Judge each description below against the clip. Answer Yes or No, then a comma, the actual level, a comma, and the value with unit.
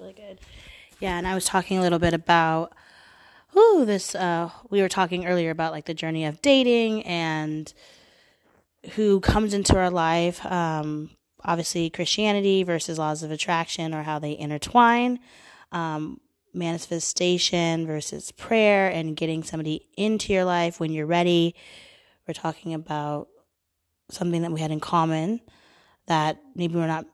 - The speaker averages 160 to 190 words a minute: No, average, 150 wpm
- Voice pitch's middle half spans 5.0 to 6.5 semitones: No, average, 3.0 semitones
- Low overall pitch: No, medium, 170 Hz